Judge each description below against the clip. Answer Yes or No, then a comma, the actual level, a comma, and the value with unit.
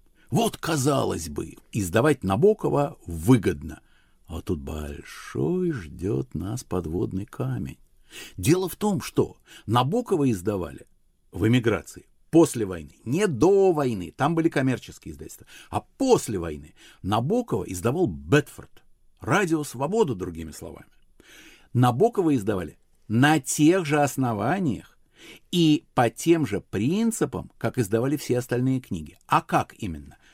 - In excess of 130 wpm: No, average, 115 wpm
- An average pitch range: No, wide, 9.0 semitones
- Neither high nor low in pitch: No, low, 125 Hz